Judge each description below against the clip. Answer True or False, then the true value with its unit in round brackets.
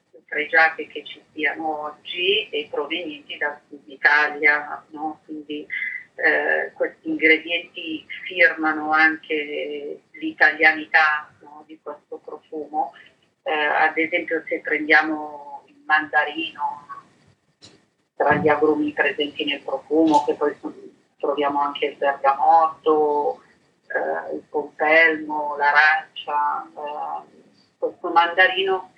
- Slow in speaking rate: True (100 wpm)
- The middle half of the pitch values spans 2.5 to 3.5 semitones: False (3.9 semitones)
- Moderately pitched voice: True (155 Hz)